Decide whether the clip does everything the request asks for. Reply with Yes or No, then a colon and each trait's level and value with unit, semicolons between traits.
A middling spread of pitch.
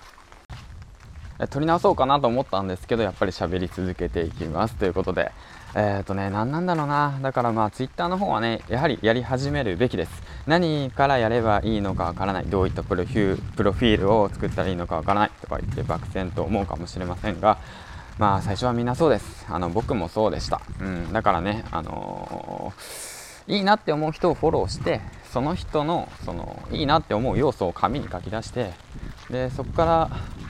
No: wide, 5.9 semitones